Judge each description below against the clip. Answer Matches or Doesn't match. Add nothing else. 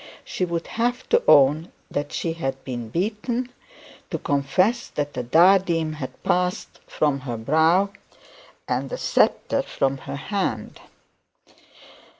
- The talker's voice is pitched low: Doesn't match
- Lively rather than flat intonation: Matches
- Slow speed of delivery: Matches